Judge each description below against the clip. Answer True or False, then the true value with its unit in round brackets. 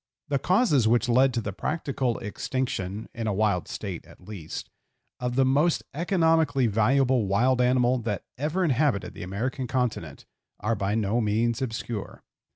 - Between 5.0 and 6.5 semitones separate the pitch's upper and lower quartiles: False (4.0 semitones)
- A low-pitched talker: True (120 Hz)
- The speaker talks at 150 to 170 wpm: True (155 wpm)